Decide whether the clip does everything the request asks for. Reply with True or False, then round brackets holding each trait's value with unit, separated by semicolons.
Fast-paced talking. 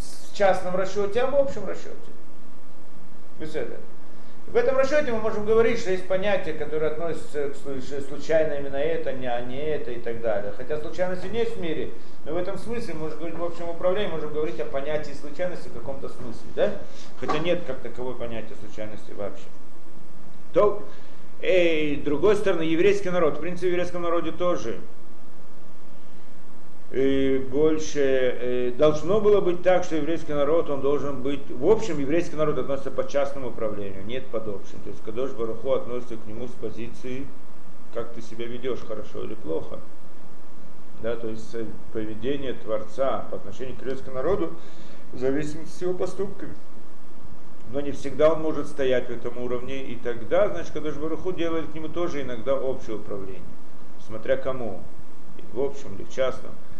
True (165 wpm)